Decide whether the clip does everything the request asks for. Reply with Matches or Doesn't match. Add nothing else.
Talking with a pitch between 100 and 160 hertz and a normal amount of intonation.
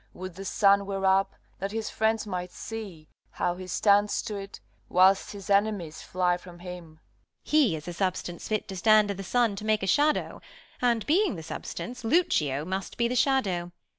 Doesn't match